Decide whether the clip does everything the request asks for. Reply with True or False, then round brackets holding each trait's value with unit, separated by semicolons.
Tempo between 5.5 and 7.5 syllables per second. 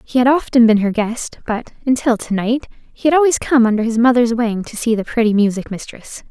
True (5.6 syllables/s)